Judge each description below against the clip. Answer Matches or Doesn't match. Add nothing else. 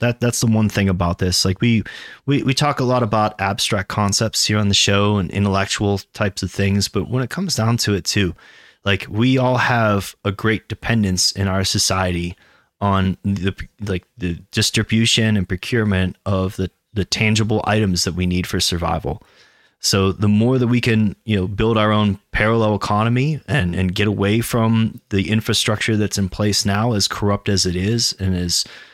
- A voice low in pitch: Matches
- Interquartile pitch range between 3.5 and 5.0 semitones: Doesn't match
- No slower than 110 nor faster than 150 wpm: Doesn't match